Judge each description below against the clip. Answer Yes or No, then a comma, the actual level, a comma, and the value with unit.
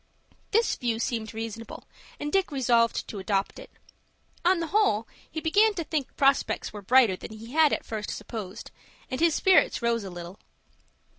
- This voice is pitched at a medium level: No, high, 235 Hz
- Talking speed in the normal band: Yes, average, 170 wpm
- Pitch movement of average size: No, wide, 6.6 semitones